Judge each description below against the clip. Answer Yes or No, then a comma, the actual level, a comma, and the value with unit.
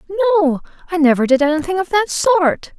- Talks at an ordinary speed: Yes, average, 175 wpm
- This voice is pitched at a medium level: No, very high, 340 Hz